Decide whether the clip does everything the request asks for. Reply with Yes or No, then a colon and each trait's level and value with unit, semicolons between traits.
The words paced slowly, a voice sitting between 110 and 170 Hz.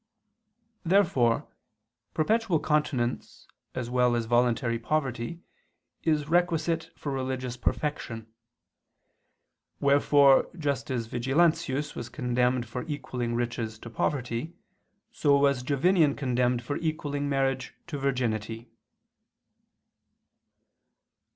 Yes: slow, 95 wpm; low, 135 Hz